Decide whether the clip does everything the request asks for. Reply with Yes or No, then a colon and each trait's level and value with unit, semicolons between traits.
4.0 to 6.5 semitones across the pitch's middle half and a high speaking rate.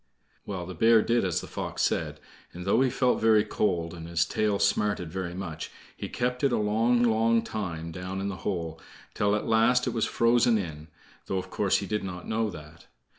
Yes: average, 4.3 semitones; fast, 210 wpm